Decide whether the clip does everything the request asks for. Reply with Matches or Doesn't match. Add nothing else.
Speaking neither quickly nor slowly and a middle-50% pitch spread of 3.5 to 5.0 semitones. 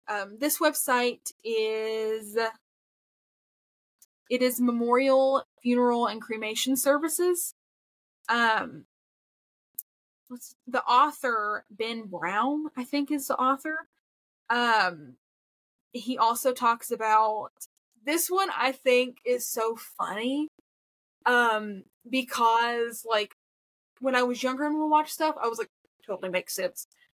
Doesn't match